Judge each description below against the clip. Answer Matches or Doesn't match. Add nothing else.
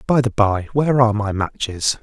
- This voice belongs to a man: Matches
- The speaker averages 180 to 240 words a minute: Matches